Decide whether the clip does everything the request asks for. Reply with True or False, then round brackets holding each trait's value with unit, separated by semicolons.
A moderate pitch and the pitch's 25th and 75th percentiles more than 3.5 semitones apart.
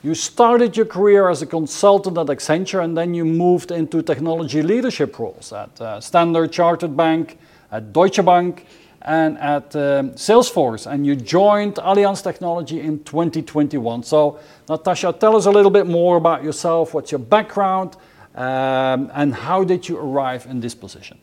True (165 Hz; 3.9 semitones)